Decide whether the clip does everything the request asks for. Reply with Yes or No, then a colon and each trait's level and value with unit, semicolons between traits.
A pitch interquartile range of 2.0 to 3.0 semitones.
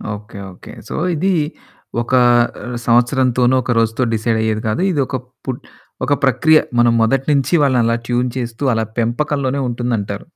Yes: narrow, 2.5 semitones